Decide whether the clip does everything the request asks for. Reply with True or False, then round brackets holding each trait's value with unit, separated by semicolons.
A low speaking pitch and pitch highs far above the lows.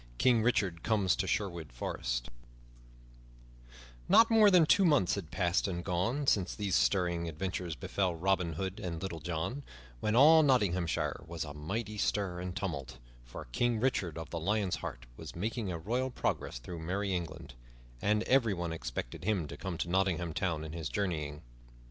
False (90 Hz; 4.4 semitones)